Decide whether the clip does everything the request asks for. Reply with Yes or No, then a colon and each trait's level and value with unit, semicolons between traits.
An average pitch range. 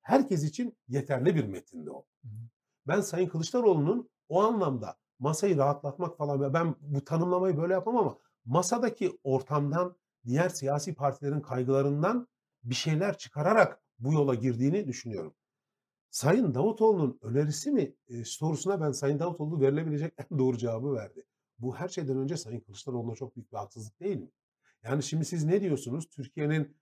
Yes: average, 4.9 semitones